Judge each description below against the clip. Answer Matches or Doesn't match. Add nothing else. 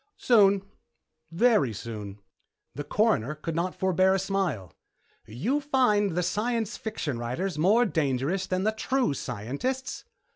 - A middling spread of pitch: Doesn't match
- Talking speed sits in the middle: Doesn't match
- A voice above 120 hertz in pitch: Matches